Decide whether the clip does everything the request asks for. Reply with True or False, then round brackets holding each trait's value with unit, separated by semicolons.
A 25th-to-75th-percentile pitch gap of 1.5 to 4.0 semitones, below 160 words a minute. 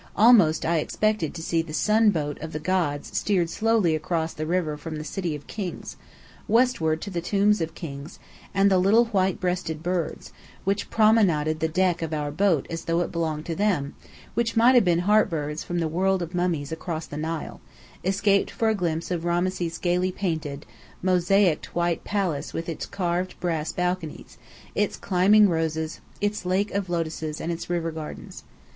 False (3.4 semitones; 180 wpm)